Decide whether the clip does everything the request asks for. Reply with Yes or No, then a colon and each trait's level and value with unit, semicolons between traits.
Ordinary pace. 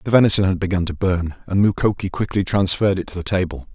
No: fast, 225 wpm